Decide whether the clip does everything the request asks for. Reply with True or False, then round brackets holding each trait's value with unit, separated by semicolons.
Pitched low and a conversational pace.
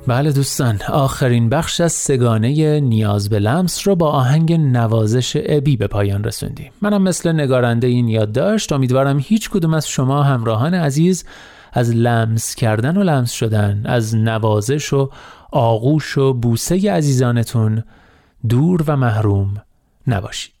True (130 Hz; 140 wpm)